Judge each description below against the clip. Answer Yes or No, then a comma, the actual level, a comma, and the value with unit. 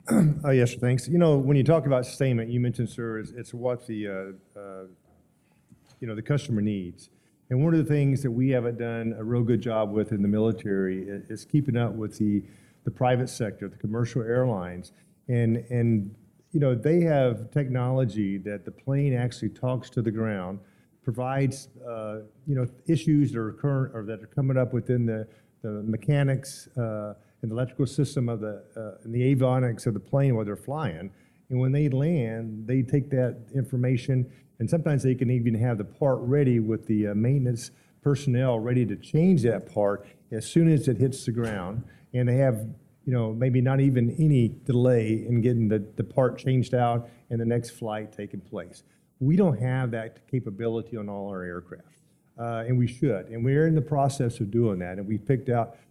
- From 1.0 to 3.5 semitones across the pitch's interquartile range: Yes, average, 3.2 semitones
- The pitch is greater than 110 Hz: Yes, low, 120 Hz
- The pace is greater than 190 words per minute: Yes, average, 200 wpm